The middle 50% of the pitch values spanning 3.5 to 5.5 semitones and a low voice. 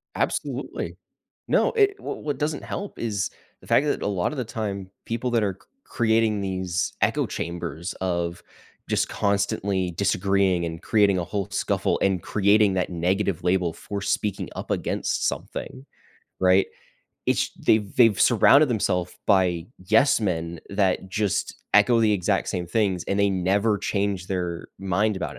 No: average, 2.9 semitones; low, 100 Hz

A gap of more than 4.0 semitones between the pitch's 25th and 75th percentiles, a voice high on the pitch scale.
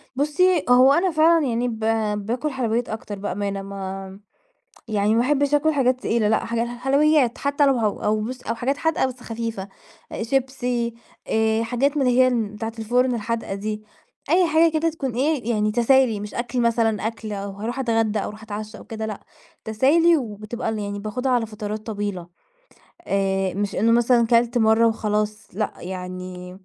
No: average, 3.5 semitones; high, 230 Hz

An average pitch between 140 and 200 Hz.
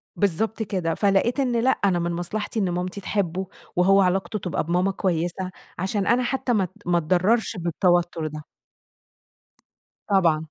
Yes: medium, 185 Hz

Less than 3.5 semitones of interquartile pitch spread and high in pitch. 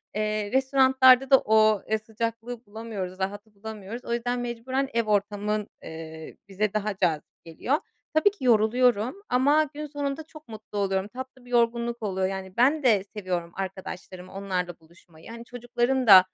No: average, 4.2 semitones; high, 220 Hz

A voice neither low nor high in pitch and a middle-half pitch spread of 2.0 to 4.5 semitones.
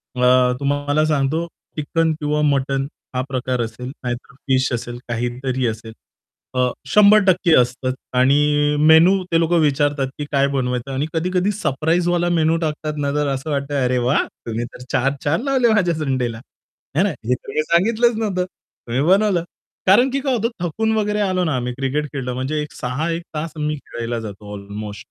No: medium, 145 Hz; average, 5.0 semitones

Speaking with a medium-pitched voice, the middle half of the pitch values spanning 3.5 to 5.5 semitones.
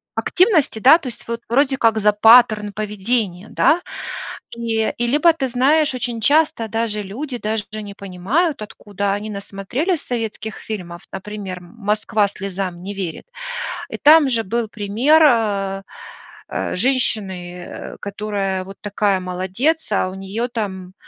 No: high, 215 Hz; average, 4.0 semitones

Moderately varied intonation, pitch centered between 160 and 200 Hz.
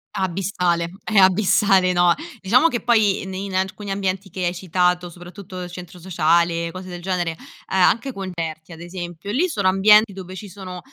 No: narrow, 1.9 semitones; medium, 185 Hz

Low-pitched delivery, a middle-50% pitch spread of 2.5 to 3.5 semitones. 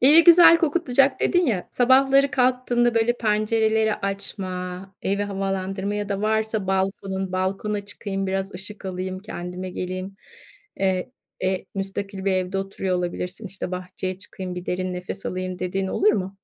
No: high, 195 Hz; average, 2.8 semitones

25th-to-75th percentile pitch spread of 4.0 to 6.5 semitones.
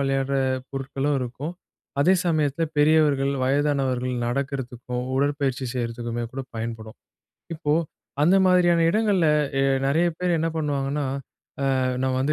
No: average, 3.0 semitones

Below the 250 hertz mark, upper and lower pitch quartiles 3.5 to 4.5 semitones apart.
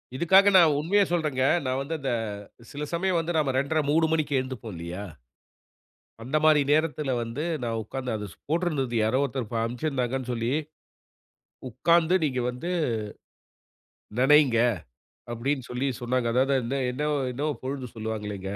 Yes: low, 135 Hz; average, 4.1 semitones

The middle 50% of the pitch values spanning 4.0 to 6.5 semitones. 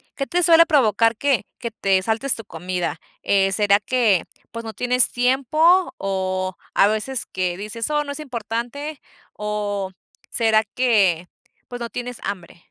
Yes: average, 4.5 semitones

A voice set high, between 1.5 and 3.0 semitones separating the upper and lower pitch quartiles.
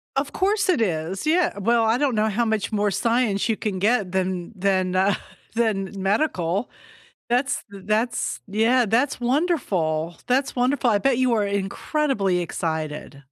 No: high, 215 Hz; average, 4.7 semitones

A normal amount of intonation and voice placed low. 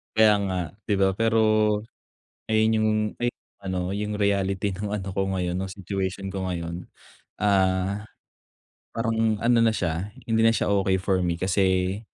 No: narrow, 2.3 semitones; very low, 95 Hz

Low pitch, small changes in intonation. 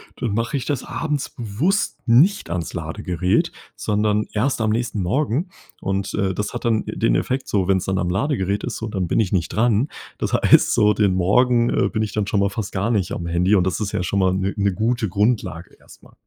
No: low, 105 Hz; average, 3.8 semitones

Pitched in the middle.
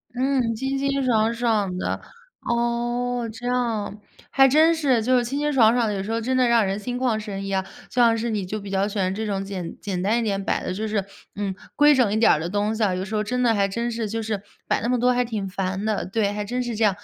No: high, 225 Hz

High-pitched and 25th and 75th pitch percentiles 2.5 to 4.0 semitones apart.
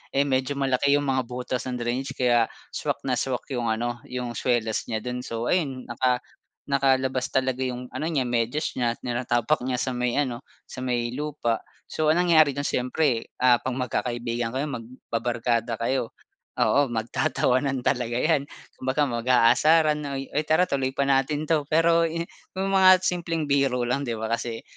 No: low, 130 Hz; average, 2.9 semitones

